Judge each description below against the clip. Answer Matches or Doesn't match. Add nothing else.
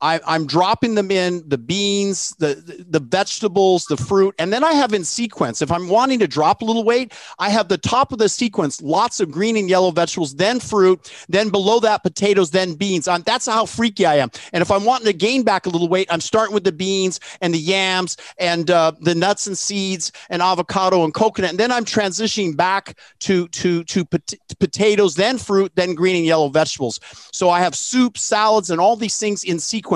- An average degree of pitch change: Matches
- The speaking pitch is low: Doesn't match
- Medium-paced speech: Doesn't match